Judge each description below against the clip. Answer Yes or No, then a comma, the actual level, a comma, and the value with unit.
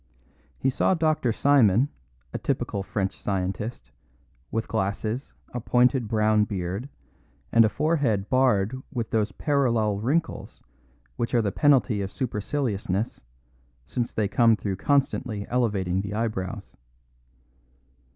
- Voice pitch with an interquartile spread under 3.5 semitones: No, average, 4.3 semitones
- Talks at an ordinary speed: No, slow, 120 wpm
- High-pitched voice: No, low, 110 Hz